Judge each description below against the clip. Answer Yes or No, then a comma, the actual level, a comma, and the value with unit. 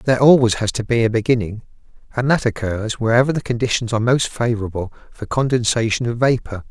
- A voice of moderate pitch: No, low, 115 Hz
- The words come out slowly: No, average, 180 wpm